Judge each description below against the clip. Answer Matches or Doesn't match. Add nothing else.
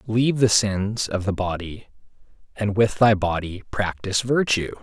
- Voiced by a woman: Doesn't match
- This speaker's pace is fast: Doesn't match